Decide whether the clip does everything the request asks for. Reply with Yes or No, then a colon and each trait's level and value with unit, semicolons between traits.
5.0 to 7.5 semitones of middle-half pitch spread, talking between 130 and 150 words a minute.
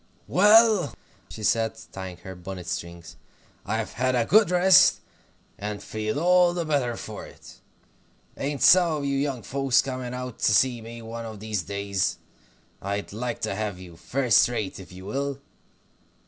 No: wide, 5.6 semitones; average, 160 wpm